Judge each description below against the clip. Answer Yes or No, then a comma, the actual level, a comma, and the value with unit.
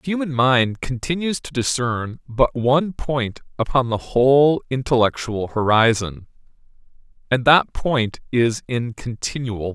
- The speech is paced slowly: Yes, slow, 130 wpm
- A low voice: Yes, low, 125 Hz